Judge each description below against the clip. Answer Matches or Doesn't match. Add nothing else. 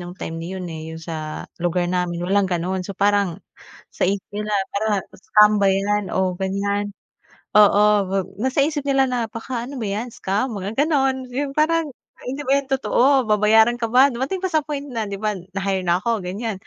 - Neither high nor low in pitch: Doesn't match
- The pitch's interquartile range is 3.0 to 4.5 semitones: Doesn't match